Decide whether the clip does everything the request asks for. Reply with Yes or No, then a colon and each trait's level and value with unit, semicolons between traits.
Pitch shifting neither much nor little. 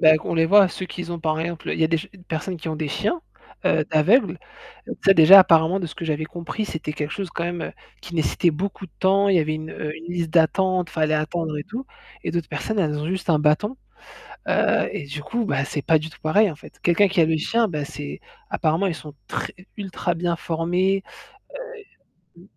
Yes: average, 3.3 semitones